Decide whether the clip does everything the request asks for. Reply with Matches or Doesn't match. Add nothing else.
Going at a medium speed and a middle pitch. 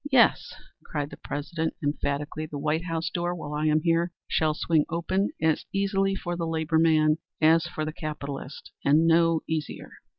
Matches